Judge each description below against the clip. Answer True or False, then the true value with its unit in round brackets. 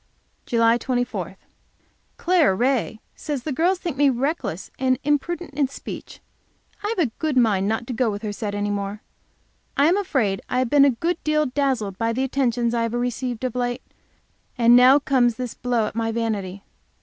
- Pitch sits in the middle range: False (245 Hz)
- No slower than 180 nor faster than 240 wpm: True (185 wpm)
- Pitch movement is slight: False (3.7 semitones)